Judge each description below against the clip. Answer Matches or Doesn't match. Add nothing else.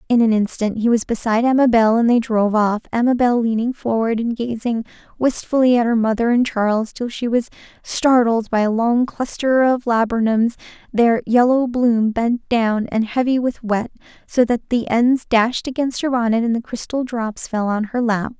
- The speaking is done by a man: Doesn't match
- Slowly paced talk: Doesn't match